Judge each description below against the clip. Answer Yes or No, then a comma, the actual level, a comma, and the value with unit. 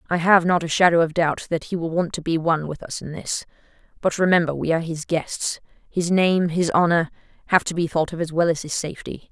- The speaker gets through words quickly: Yes, fast, 245 wpm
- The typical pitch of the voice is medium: Yes, medium, 165 Hz